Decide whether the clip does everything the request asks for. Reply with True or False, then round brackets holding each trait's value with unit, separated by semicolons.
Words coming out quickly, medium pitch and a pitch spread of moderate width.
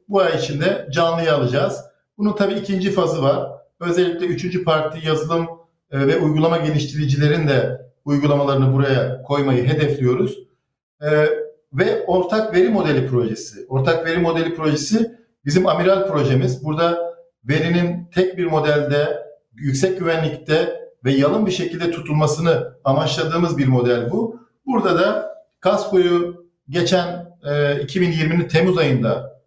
False (115 wpm; 165 Hz; 3.7 semitones)